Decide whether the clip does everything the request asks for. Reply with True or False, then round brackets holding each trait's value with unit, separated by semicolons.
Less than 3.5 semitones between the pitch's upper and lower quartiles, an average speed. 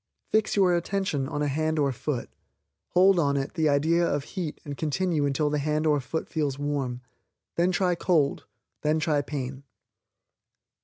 True (3.1 semitones; 165 wpm)